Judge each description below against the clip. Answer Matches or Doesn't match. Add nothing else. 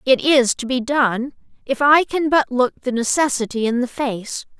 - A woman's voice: Matches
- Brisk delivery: Doesn't match